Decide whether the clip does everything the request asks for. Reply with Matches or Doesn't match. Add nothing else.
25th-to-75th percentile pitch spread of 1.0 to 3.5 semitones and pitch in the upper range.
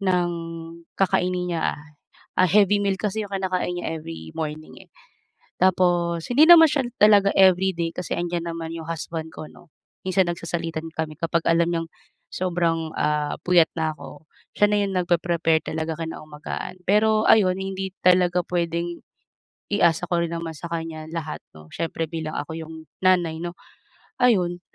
Doesn't match